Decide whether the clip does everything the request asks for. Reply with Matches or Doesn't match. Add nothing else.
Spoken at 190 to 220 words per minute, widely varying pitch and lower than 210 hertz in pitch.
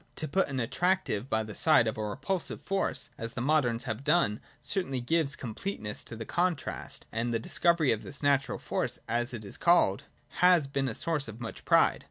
Matches